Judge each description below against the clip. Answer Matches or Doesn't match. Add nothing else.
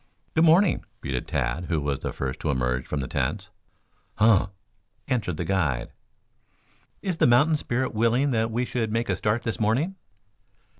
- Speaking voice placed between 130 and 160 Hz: Doesn't match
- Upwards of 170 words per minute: Doesn't match